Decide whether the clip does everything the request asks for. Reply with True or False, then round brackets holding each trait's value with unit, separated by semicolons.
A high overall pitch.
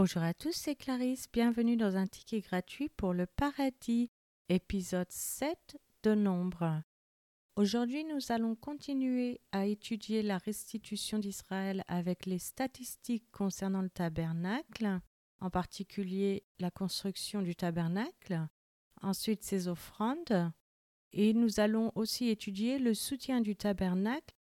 True (205 Hz)